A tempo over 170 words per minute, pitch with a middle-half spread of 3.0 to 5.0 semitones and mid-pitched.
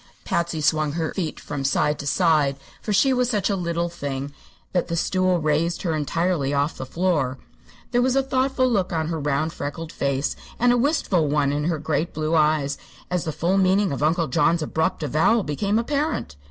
Yes: average, 195 wpm; average, 4.3 semitones; medium, 165 Hz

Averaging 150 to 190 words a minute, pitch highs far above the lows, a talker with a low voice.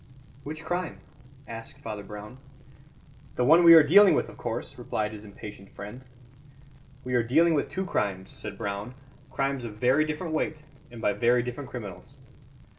Yes: average, 165 wpm; wide, 6.5 semitones; low, 125 Hz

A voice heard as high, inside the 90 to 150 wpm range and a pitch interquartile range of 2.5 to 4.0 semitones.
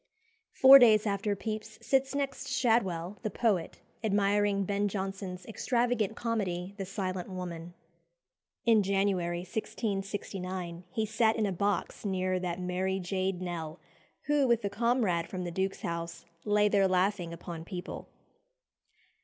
Yes: high, 195 Hz; slow, 135 wpm; average, 3.0 semitones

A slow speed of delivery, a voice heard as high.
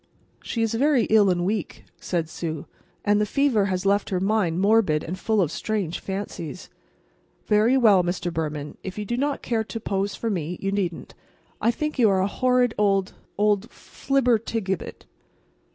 No: average, 170 wpm; high, 205 Hz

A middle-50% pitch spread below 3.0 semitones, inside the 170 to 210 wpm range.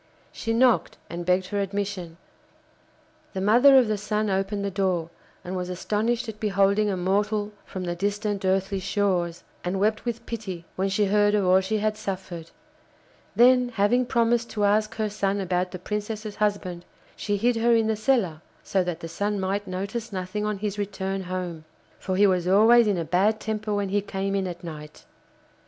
Yes: narrow, 2.4 semitones; average, 185 wpm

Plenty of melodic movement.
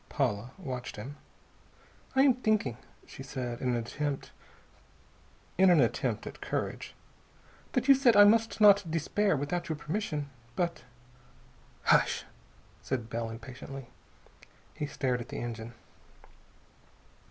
Yes: wide, 8.4 semitones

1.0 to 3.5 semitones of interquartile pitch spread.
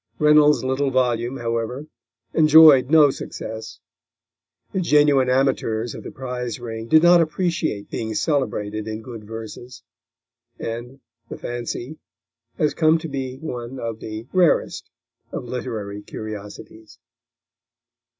No: average, 4.7 semitones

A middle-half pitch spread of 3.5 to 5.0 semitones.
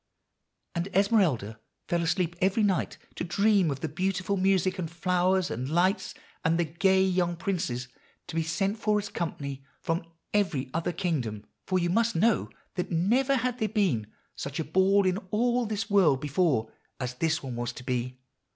Yes: average, 4.6 semitones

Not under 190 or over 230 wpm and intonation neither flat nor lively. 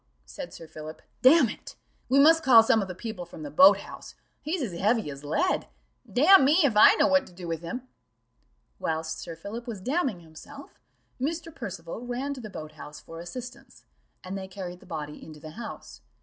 No: average, 200 wpm; wide, 8.1 semitones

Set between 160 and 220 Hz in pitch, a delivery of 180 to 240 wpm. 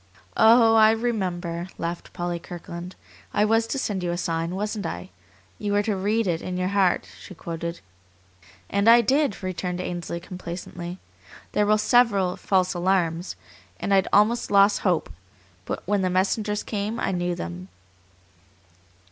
No: high, 190 Hz; average, 155 wpm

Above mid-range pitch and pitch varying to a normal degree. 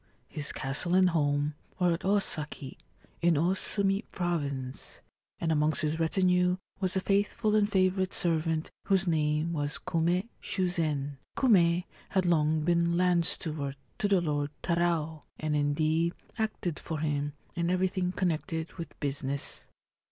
No: medium, 170 Hz; average, 3.3 semitones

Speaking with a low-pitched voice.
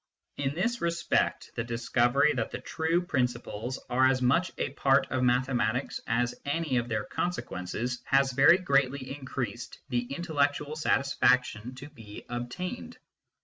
Yes: low, 130 Hz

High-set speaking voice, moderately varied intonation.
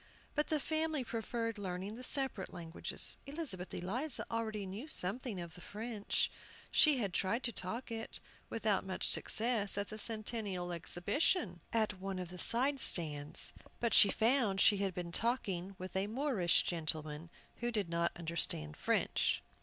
Yes: high, 205 Hz; average, 4.7 semitones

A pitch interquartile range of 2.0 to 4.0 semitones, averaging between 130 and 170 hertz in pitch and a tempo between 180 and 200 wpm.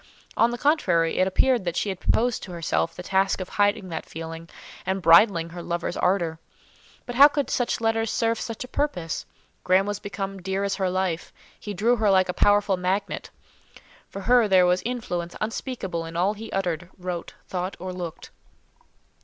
No: average, 3.5 semitones; high, 190 Hz; average, 185 wpm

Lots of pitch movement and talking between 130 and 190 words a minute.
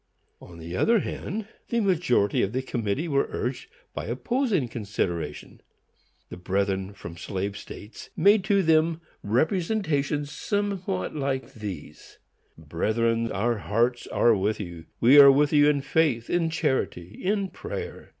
Yes: wide, 8.4 semitones; average, 140 wpm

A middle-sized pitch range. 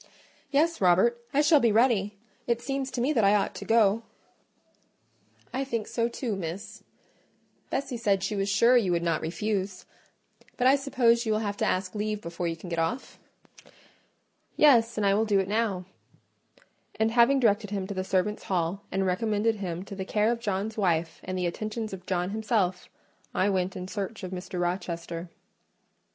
Yes: average, 3.9 semitones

